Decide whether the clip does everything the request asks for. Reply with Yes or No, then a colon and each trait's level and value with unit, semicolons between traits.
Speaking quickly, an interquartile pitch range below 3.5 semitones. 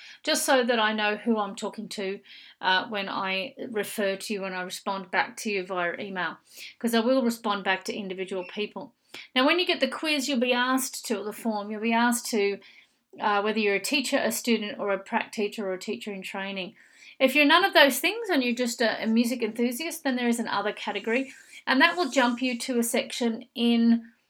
No: fast, 220 wpm; average, 4.1 semitones